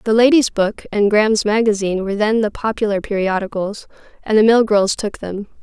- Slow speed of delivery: No, average, 180 wpm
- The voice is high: Yes, high, 210 Hz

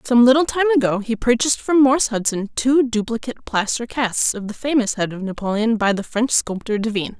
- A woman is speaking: Yes, female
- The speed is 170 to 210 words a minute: Yes, average, 200 wpm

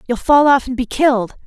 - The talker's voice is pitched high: Yes, very high, 255 Hz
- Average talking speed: No, fast, 245 wpm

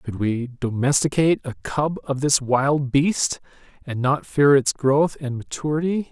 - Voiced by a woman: No, male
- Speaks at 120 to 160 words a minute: Yes, average, 155 wpm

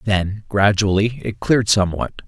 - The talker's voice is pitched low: Yes, low, 105 Hz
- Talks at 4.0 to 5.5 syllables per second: Yes, 5.2 syllables/s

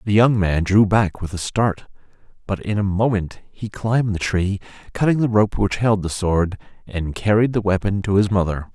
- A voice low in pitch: Yes, low, 100 Hz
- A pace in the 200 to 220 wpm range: Yes, fast, 205 wpm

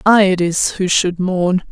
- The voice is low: No, medium, 185 Hz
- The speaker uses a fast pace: Yes, fast, 210 wpm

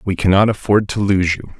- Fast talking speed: Yes, fast, 225 wpm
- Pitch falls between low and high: No, very low, 95 Hz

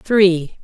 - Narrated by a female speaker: Yes, female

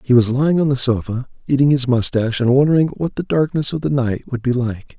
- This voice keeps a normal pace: No, fast, 240 wpm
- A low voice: Yes, low, 130 Hz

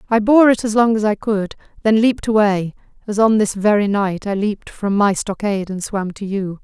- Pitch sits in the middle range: No, high, 205 Hz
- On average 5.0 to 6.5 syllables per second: Yes, 5.3 syllables/s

